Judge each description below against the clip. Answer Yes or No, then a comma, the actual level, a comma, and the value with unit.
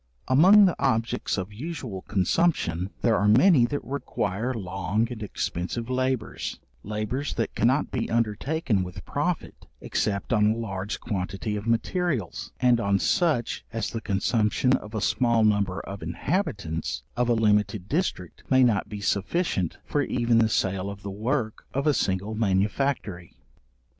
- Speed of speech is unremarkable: Yes, average, 150 wpm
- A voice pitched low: Yes, low, 110 Hz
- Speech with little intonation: No, average, 4.5 semitones